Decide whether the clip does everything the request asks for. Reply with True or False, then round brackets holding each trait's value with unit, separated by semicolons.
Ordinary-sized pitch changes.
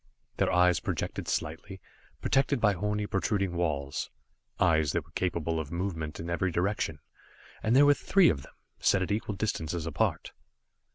True (4.4 semitones)